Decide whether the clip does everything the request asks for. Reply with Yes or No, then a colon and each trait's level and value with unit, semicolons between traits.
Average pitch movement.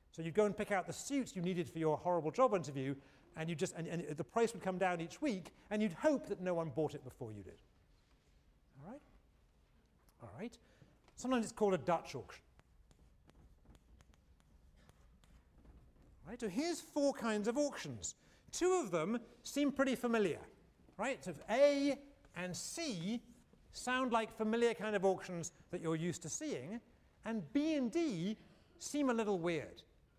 No: wide, 7.8 semitones